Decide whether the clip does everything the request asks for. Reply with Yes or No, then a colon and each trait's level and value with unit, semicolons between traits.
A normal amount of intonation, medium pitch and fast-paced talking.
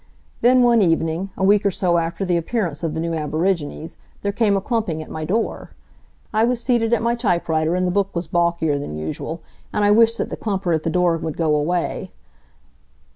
Yes: average, 4.4 semitones; medium, 180 Hz; fast, 210 wpm